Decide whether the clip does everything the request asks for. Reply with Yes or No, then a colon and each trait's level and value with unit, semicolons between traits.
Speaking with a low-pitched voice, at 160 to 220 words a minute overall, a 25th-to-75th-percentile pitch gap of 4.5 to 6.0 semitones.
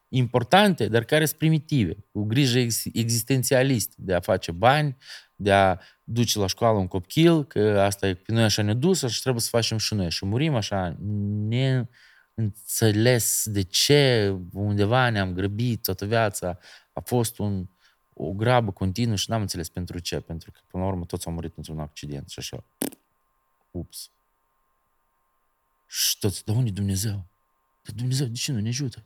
Yes: low, 110 Hz; average, 165 wpm; average, 5.2 semitones